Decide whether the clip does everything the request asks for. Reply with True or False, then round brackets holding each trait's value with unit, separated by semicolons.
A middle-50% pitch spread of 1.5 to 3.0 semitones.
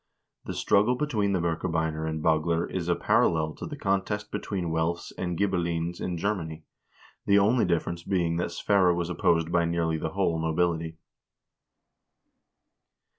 True (2.7 semitones)